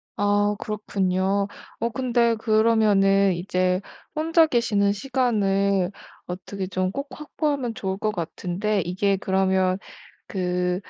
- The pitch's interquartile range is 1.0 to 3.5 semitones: Yes, average, 2.9 semitones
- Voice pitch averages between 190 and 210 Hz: Yes, high, 200 Hz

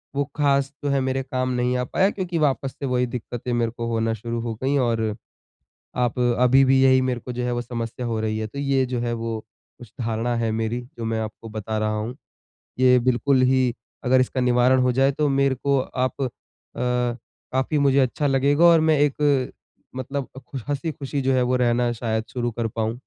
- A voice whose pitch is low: Yes, low, 125 Hz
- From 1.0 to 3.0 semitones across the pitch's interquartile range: Yes, narrow, 2.5 semitones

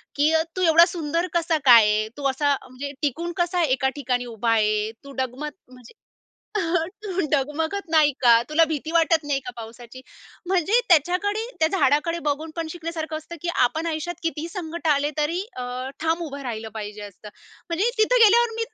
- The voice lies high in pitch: Yes, very high, 310 Hz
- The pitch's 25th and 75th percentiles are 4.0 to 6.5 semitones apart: Yes, average, 4.7 semitones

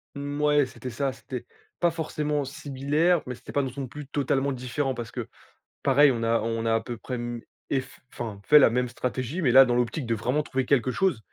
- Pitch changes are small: No, average, 3.1 semitones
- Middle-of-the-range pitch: No, low, 130 Hz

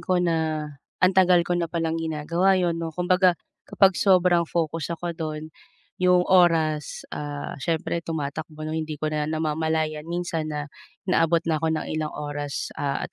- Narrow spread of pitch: Yes, narrow, 2.3 semitones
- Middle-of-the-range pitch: Yes, medium, 165 Hz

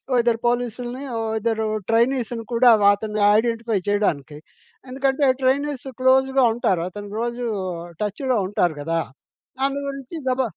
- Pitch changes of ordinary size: Yes, average, 3.6 semitones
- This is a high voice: Yes, high, 240 Hz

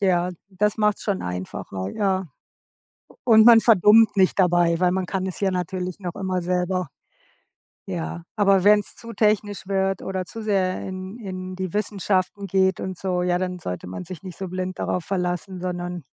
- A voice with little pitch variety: Yes, narrow, 1.8 semitones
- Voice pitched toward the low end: No, medium, 185 Hz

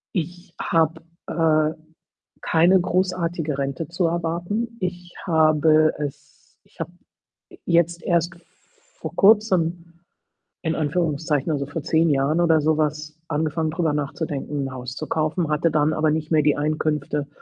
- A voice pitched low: No, medium, 160 Hz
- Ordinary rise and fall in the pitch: No, narrow, 2.2 semitones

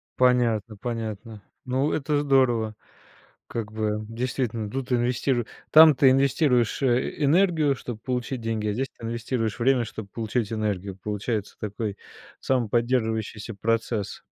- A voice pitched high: No, low, 115 Hz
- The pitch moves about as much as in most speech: Yes, average, 3.1 semitones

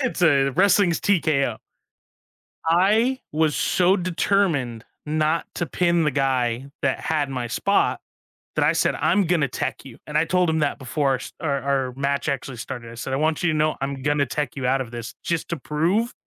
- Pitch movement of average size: Yes, average, 4.2 semitones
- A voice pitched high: No, medium, 150 Hz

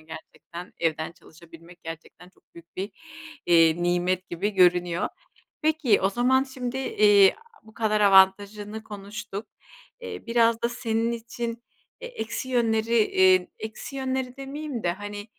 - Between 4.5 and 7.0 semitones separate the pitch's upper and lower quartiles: Yes, average, 4.8 semitones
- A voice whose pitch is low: No, high, 210 Hz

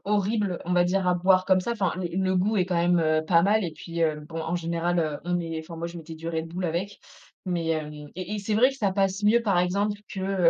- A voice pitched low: No, medium, 180 Hz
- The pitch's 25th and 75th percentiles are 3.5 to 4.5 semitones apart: No, average, 2.8 semitones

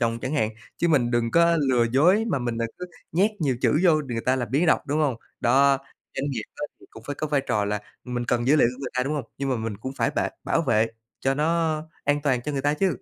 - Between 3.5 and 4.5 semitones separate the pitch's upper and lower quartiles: Yes, average, 3.8 semitones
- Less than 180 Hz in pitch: Yes, low, 135 Hz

